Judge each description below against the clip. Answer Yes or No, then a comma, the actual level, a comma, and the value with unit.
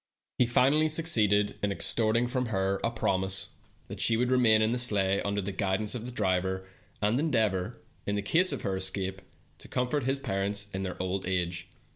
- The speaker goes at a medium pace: Yes, average, 180 wpm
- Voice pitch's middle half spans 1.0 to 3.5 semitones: No, average, 4.3 semitones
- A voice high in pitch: No, low, 105 Hz